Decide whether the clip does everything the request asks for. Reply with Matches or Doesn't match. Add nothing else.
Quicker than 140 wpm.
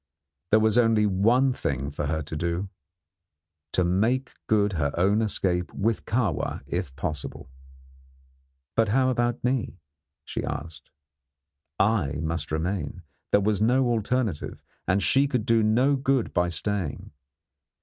Doesn't match